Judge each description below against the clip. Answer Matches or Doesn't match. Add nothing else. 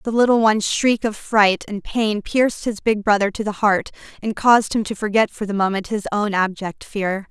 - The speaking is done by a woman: Matches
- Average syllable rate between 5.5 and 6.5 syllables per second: Doesn't match